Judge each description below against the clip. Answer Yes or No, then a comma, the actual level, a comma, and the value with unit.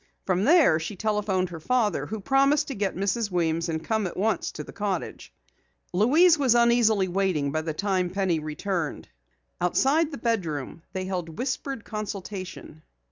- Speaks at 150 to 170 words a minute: Yes, average, 160 wpm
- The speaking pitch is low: No, high, 195 Hz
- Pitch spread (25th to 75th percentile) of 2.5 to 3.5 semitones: No, average, 5.0 semitones